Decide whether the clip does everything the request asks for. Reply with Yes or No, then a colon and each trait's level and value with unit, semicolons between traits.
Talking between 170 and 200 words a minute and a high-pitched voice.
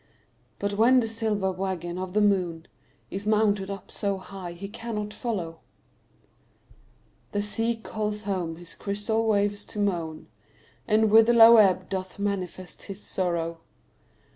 No: average, 140 wpm; high, 200 Hz